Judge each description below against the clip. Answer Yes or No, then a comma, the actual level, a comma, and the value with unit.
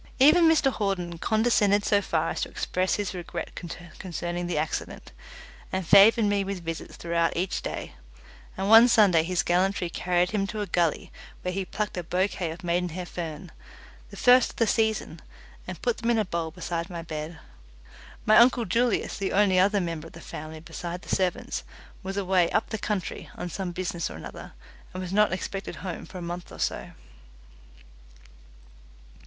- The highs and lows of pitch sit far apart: No, average, 3.1 semitones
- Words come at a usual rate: Yes, average, 180 wpm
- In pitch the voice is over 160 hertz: Yes, medium, 185 Hz